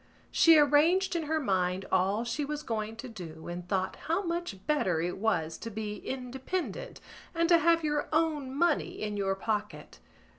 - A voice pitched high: Yes, very high, 250 Hz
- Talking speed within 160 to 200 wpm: Yes, average, 175 wpm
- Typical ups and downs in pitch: No, wide, 8.5 semitones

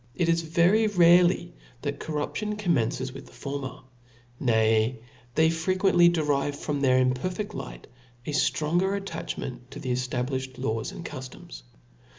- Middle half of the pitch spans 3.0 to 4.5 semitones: No, average, 5.1 semitones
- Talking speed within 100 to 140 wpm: Yes, slow, 135 wpm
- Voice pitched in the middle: Yes, medium, 145 Hz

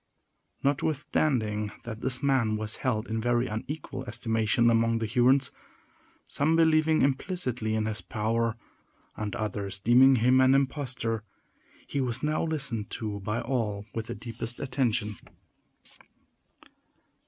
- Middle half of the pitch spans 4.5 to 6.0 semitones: No, average, 3.5 semitones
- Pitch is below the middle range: Yes, low, 120 Hz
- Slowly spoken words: Yes, slow, 120 wpm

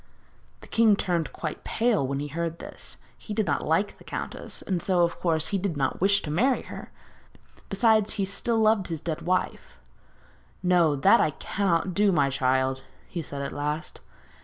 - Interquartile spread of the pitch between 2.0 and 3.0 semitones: No, average, 5.1 semitones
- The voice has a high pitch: No, medium, 175 Hz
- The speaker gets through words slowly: No, average, 185 wpm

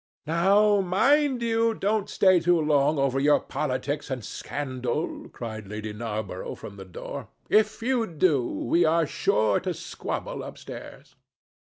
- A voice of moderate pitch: Yes, medium, 155 Hz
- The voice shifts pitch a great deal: Yes, wide, 8.6 semitones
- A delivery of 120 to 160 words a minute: Yes, average, 140 wpm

